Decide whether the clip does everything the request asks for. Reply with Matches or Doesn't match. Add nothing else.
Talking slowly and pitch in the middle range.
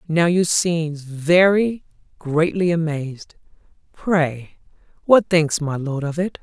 Matches